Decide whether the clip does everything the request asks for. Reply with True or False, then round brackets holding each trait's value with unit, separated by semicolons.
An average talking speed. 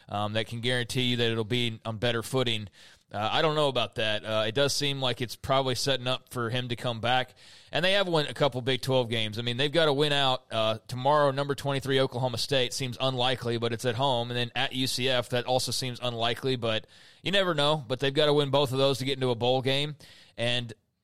False (245 wpm)